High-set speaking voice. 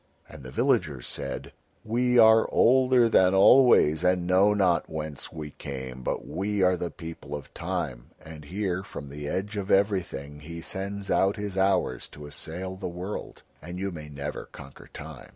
No: very low, 90 Hz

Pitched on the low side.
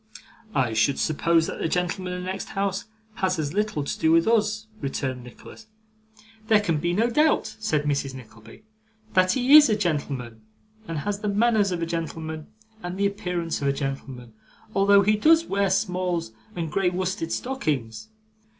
No: medium, 180 Hz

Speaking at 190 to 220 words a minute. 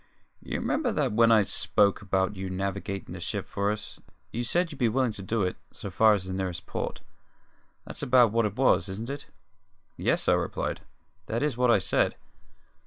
Yes: average, 195 wpm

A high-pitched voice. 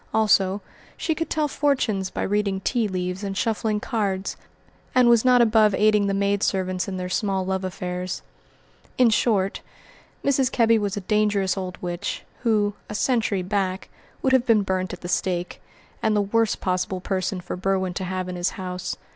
Yes: high, 200 Hz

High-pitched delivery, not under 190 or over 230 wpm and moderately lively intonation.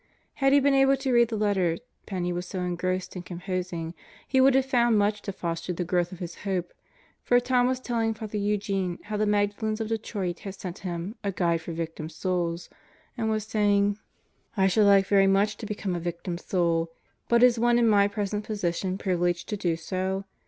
Yes: high, 200 Hz; average, 200 wpm; average, 3.6 semitones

